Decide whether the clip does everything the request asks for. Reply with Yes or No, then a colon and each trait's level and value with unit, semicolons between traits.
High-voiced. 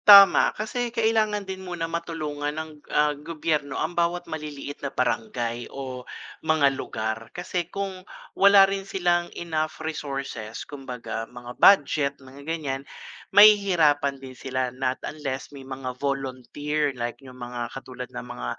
No: medium, 145 Hz